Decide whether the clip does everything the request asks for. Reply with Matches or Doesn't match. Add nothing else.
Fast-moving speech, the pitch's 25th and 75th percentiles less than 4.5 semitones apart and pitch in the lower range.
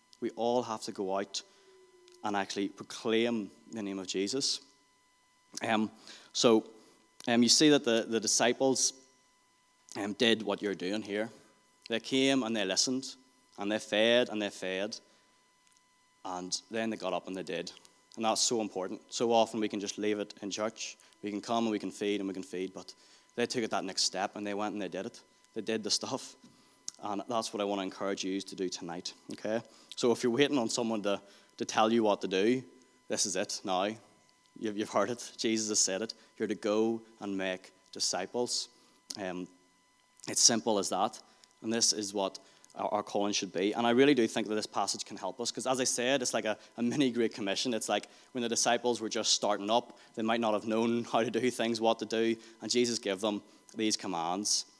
Matches